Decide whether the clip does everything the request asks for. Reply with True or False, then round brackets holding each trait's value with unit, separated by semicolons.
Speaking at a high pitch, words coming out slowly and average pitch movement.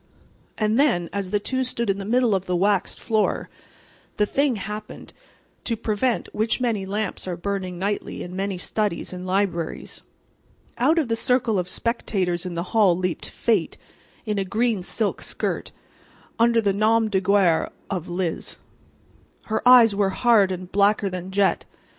False (200 Hz; 165 wpm; 3.4 semitones)